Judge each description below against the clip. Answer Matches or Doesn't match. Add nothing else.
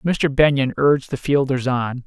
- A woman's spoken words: Doesn't match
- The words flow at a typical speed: Matches